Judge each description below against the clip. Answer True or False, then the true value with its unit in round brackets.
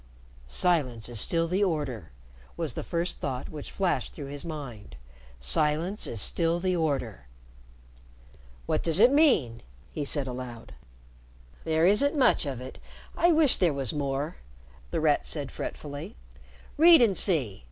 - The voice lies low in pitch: False (155 Hz)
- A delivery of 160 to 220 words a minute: False (145 wpm)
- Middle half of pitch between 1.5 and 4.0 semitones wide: False (5.6 semitones)